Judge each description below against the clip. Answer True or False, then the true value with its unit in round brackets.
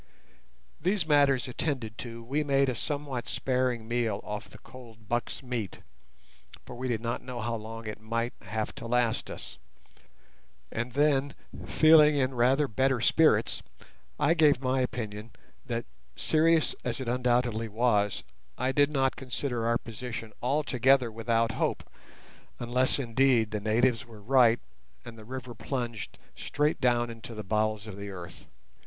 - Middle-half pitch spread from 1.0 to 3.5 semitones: True (2.8 semitones)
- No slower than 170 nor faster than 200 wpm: False (150 wpm)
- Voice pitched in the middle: False (120 Hz)